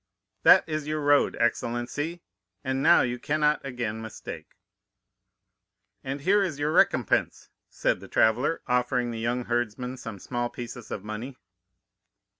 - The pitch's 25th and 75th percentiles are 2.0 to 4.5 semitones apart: Yes, average, 3.5 semitones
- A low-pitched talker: Yes, low, 125 Hz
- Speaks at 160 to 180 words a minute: No, slow, 135 wpm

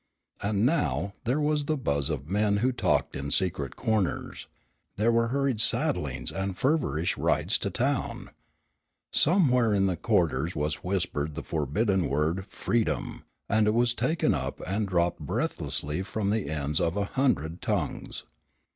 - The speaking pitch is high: No, low, 100 Hz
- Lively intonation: Yes, wide, 6.5 semitones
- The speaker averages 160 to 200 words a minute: No, average, 150 wpm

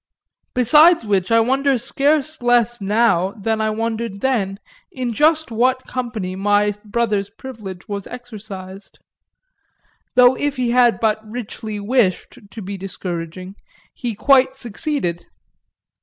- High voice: Yes, high, 225 Hz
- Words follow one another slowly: Yes, slow, 125 wpm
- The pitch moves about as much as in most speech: Yes, average, 4.0 semitones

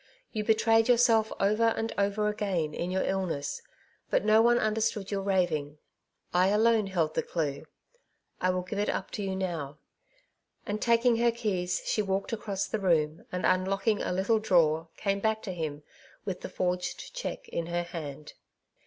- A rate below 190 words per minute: Yes, average, 175 wpm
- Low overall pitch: No, high, 195 Hz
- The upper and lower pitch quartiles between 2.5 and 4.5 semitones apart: Yes, average, 3.8 semitones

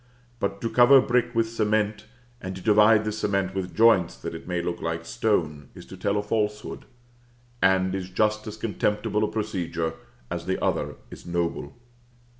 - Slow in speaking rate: No, average, 175 wpm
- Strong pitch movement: No, average, 3.0 semitones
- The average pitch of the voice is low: Yes, low, 105 Hz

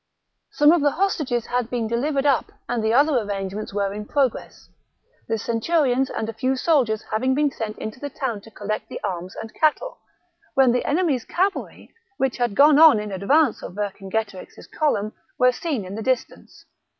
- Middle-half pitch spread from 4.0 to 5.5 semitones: Yes, average, 5.2 semitones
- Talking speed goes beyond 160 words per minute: Yes, average, 180 wpm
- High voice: Yes, high, 245 Hz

